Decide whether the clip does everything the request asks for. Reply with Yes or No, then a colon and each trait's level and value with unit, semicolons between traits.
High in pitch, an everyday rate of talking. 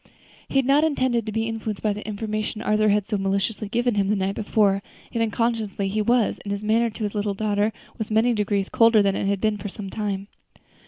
No: high, 215 Hz; fast, 225 wpm